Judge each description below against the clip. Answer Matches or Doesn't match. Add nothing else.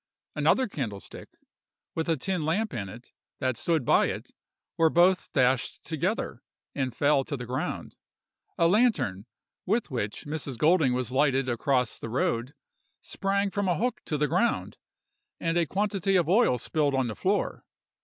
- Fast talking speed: Doesn't match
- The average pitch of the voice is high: Doesn't match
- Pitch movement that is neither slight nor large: Doesn't match